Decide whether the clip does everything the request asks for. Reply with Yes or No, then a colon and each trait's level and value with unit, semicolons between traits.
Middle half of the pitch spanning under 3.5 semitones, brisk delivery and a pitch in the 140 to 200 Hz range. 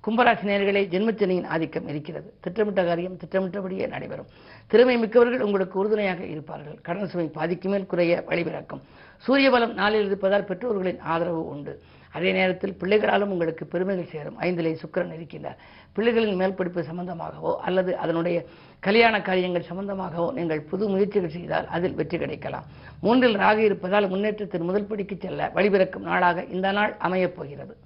Yes: average, 2.9 semitones; fast, 135 wpm; medium, 185 Hz